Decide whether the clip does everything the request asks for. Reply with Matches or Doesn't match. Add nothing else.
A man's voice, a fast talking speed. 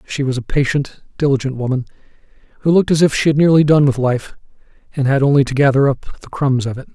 Matches